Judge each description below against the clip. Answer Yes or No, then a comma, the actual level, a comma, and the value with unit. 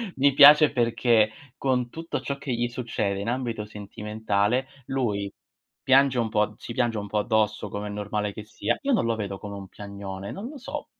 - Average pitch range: Yes, average, 3.8 semitones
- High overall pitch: No, low, 110 Hz